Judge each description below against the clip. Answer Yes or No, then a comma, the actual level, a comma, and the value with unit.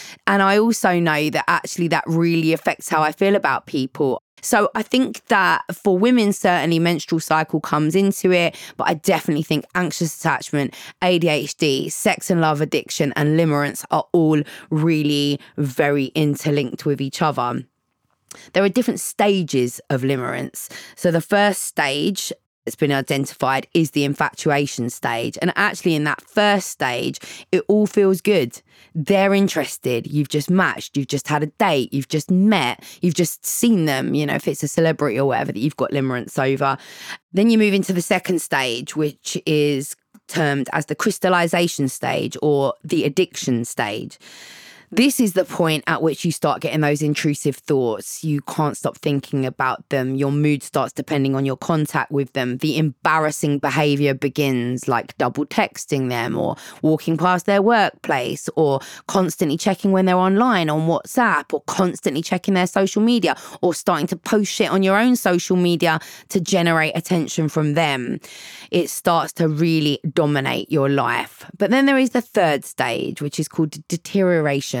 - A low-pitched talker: No, medium, 160 Hz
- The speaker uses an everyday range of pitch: Yes, average, 4.4 semitones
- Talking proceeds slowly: No, average, 170 wpm